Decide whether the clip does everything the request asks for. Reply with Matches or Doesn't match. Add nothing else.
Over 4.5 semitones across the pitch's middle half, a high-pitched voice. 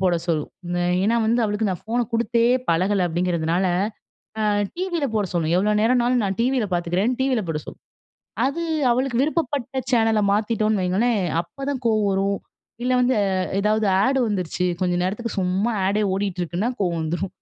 Matches